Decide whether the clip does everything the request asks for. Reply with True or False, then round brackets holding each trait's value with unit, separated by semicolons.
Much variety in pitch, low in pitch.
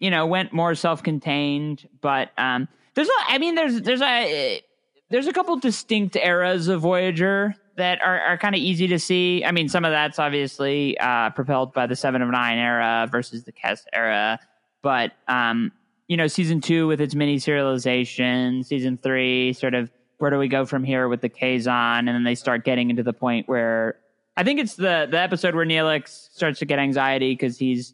False (6.1 semitones; 145 Hz)